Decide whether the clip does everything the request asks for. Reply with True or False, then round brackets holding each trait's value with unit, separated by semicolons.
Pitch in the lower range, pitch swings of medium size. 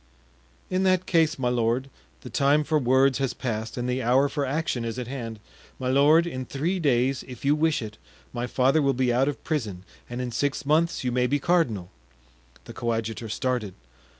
True (130 Hz; 3.3 semitones)